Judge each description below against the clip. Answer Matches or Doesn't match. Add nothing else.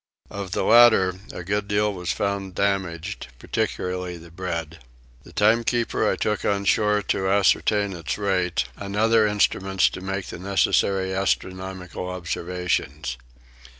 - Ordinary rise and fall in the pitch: Doesn't match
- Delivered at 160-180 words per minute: Doesn't match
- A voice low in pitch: Matches